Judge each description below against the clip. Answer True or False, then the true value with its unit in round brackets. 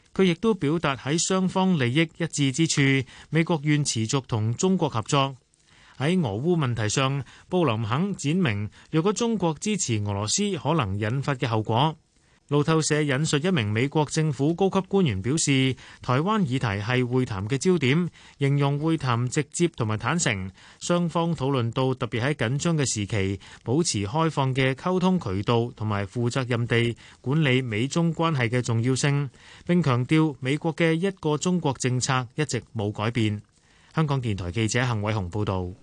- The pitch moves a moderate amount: False (5.7 semitones)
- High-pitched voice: False (140 Hz)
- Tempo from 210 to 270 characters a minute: True (260 characters per minute)